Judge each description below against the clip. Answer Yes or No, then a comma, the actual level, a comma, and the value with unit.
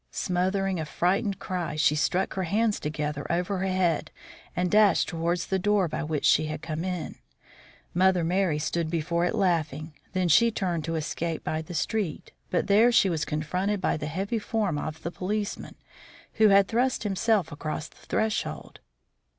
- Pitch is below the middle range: No, medium, 180 Hz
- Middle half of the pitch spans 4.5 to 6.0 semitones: No, average, 3.9 semitones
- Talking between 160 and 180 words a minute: Yes, average, 175 wpm